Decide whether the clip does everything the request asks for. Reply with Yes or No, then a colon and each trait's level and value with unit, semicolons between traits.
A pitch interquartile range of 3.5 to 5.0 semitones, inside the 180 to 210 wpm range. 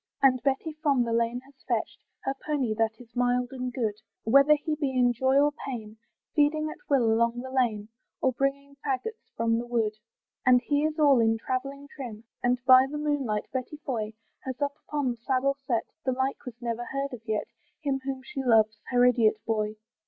No: average, 3.0 semitones; average, 195 wpm